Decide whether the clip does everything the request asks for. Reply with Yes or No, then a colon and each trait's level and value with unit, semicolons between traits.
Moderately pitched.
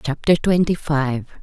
Yes: medium, 150 Hz